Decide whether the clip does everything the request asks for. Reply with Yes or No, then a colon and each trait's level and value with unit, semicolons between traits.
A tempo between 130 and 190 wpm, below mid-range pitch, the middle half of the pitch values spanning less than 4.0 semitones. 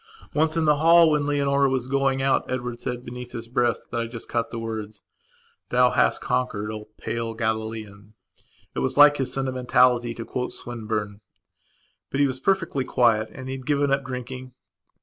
Yes: average, 175 wpm; low, 125 Hz; average, 3.2 semitones